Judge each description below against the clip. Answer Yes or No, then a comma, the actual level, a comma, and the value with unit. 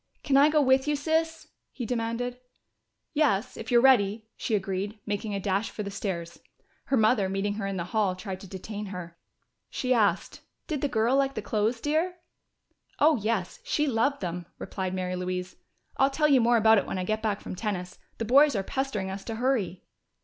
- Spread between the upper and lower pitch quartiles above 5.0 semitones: Yes, wide, 5.4 semitones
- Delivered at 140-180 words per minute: No, average, 200 wpm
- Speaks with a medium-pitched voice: No, high, 220 Hz